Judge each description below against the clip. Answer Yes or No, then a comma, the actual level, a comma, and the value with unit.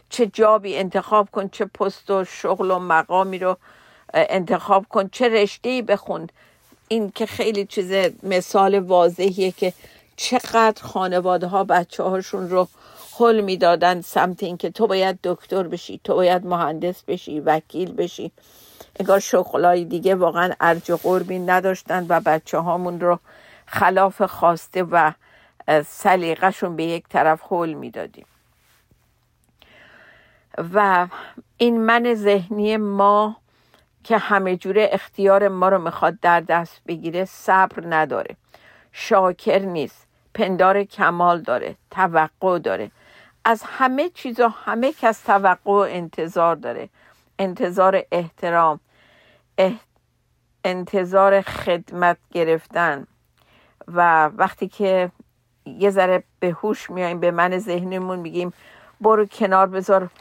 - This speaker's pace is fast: No, average, 120 wpm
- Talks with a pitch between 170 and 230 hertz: Yes, high, 190 Hz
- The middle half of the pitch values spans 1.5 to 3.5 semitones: Yes, narrow, 2.5 semitones